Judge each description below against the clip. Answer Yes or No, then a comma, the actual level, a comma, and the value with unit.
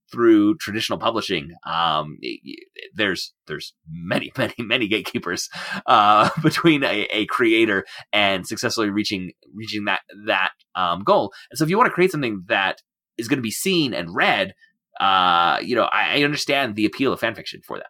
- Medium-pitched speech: Yes, medium, 150 Hz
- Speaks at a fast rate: No, average, 180 wpm